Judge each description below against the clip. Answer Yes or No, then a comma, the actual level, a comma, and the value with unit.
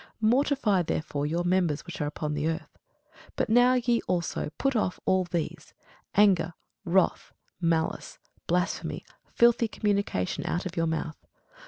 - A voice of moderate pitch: Yes, medium, 180 Hz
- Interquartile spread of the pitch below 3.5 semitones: No, average, 4.6 semitones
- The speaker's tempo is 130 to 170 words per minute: Yes, average, 140 wpm